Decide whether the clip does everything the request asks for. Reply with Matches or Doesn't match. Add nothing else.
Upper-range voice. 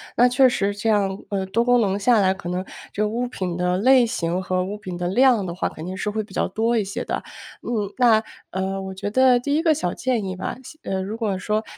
Matches